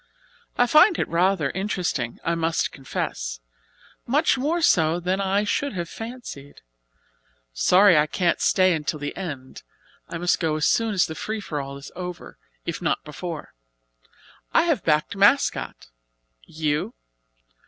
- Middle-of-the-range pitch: Yes, medium, 175 Hz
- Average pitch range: Yes, average, 5.0 semitones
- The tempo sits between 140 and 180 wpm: Yes, average, 145 wpm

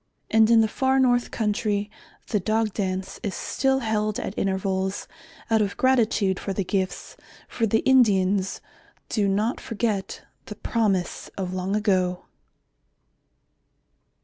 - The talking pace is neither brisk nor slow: No, slow, 130 wpm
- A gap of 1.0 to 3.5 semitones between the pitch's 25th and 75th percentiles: Yes, average, 2.8 semitones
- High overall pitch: Yes, high, 210 Hz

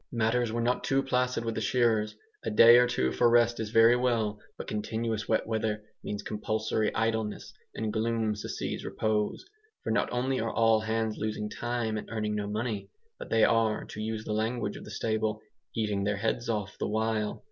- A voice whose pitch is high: No, low, 110 Hz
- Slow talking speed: No, average, 190 wpm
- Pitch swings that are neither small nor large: No, narrow, 1.5 semitones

